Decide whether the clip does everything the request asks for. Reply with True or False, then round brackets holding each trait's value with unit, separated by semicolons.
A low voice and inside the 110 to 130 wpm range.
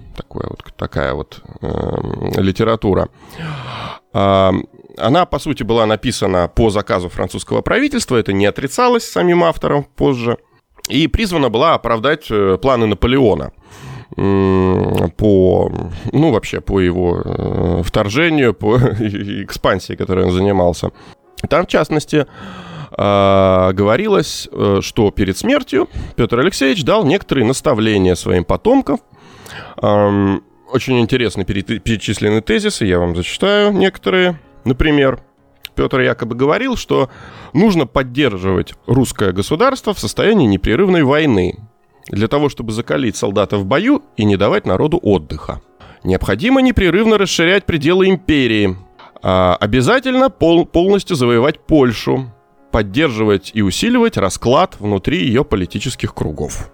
True (110 Hz; 115 wpm)